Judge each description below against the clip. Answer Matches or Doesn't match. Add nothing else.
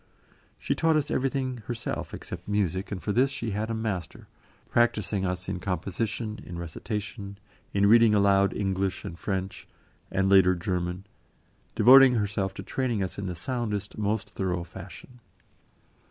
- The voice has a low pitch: Matches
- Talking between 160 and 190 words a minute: Doesn't match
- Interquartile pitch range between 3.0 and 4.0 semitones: Matches